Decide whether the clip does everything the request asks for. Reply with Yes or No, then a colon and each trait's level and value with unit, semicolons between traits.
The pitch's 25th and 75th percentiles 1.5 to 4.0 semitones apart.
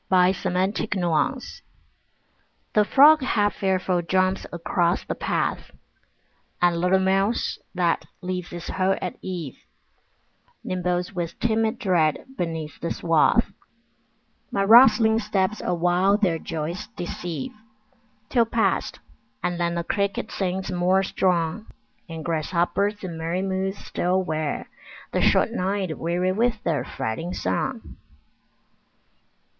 Yes: average, 2.7 semitones